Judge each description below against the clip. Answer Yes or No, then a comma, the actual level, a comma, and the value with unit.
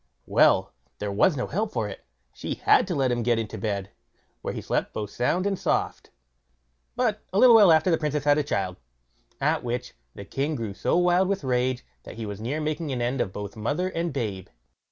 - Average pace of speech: No, fast, 215 wpm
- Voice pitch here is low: Yes, low, 130 Hz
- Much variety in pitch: Yes, wide, 7.1 semitones